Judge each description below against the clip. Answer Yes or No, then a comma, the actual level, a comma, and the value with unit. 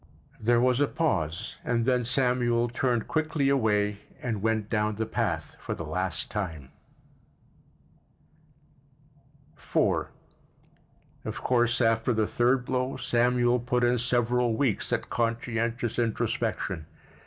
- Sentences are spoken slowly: Yes, slow, 120 wpm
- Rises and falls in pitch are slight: Yes, narrow, 2.2 semitones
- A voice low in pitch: Yes, low, 120 Hz